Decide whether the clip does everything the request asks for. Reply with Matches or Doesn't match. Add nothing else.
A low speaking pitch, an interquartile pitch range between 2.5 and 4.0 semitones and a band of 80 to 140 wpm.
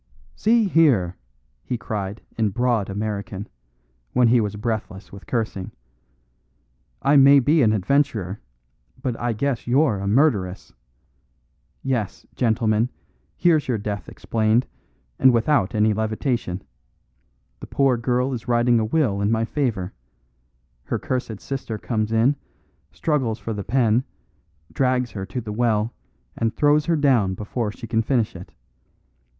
Matches